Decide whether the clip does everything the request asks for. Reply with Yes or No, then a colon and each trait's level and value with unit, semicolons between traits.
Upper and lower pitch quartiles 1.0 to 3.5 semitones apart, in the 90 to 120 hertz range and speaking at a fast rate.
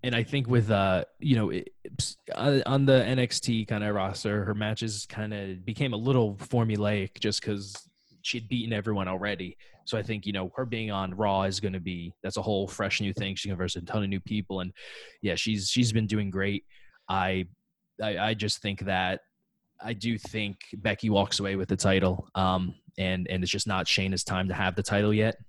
Yes: narrow, 2.5 semitones; low, 105 Hz; fast, 210 wpm